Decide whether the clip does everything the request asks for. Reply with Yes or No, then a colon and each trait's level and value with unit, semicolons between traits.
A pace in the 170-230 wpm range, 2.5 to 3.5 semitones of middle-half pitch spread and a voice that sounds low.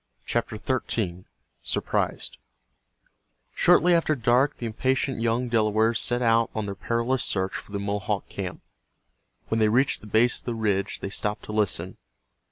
No: average, 150 wpm; average, 2.9 semitones; low, 110 Hz